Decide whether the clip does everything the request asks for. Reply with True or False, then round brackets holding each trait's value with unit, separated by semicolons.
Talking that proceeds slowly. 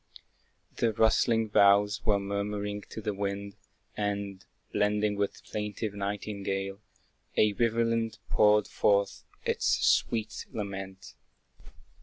True (105 wpm)